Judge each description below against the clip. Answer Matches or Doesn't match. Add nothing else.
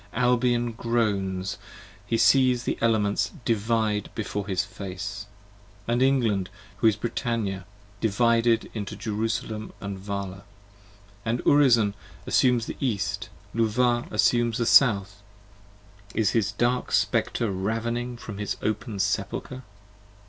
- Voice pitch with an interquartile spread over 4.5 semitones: Doesn't match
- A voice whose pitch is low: Matches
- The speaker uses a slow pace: Matches